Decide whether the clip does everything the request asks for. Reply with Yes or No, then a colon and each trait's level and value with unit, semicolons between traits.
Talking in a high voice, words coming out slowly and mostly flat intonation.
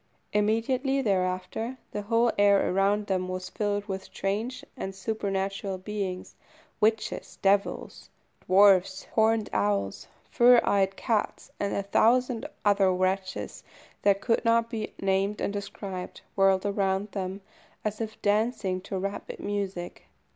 Yes: high, 200 Hz; slow, 125 wpm; narrow, 2.3 semitones